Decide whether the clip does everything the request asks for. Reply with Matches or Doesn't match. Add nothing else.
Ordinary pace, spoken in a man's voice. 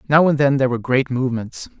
Doesn't match